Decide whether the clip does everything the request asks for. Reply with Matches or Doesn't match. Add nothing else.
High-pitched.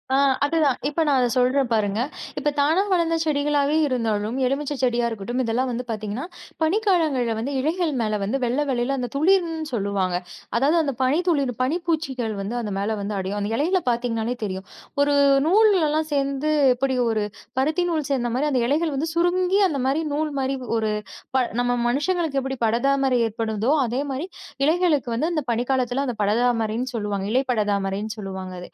Matches